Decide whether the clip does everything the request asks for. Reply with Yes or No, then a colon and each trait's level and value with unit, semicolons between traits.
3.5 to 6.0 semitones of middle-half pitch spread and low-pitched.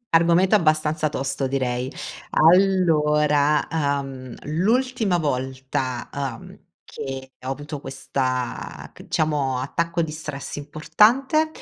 No: average, 4.0 semitones; medium, 150 Hz